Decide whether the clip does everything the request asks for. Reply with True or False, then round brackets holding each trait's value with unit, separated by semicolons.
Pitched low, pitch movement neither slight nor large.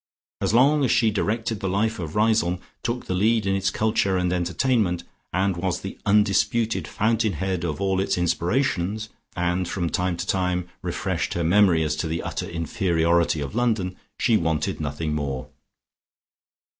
True (95 Hz; 4.0 semitones)